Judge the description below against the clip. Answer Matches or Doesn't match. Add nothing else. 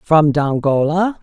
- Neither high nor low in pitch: Matches